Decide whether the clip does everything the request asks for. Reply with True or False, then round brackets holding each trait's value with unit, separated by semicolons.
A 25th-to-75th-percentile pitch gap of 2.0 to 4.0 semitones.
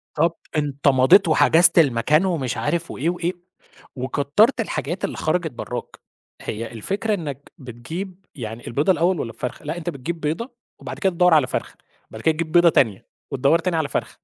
False (4.9 semitones)